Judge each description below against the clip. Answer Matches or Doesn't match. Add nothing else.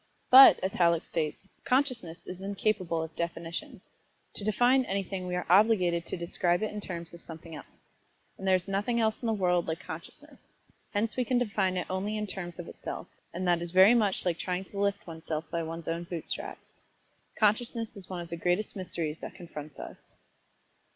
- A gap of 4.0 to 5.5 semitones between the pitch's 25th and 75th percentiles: Doesn't match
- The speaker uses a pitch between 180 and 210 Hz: Matches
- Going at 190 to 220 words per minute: Matches